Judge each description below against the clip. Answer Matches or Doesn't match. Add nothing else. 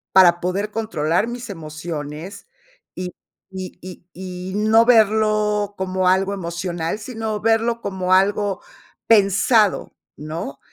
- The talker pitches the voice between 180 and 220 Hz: Matches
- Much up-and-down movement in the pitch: Doesn't match